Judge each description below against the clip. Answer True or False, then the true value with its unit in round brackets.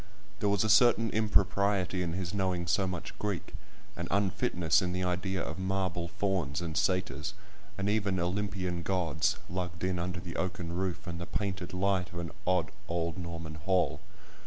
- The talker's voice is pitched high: False (90 Hz)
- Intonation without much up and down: True (2.1 semitones)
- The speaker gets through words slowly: False (165 wpm)